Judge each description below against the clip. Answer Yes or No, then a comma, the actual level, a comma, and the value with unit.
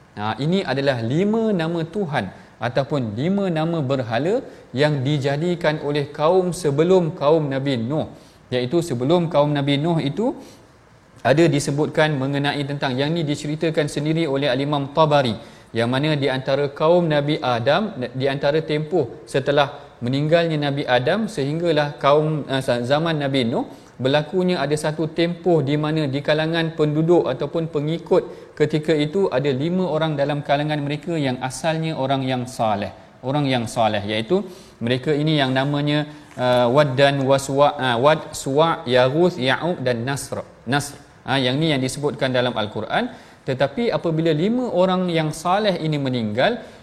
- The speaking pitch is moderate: Yes, medium, 145 Hz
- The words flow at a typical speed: No, fast, 145 wpm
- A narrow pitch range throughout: No, average, 3.2 semitones